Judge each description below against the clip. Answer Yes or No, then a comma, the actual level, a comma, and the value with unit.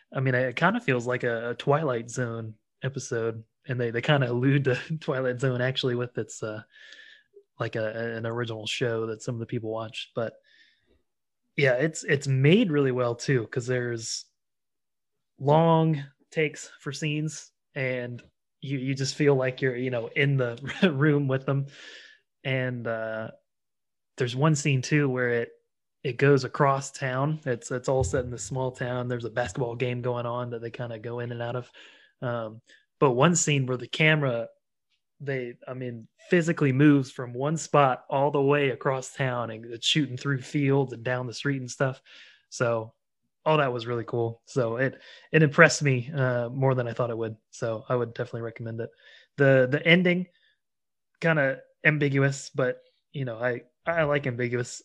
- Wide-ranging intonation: No, average, 3.3 semitones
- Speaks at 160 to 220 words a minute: Yes, average, 180 wpm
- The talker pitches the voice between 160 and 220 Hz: No, low, 130 Hz